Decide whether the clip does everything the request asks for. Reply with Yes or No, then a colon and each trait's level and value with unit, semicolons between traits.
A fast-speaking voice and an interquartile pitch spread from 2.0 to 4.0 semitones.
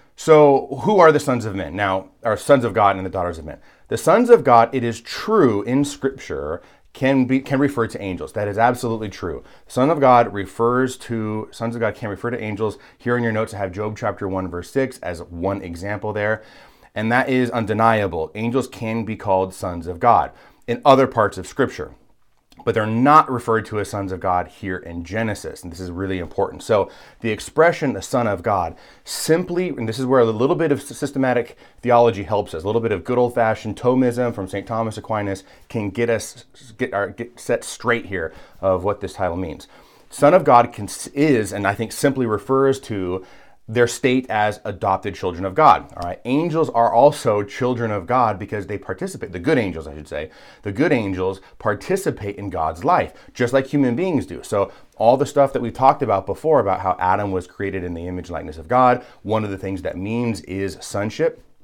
No: fast, 210 wpm; average, 4.6 semitones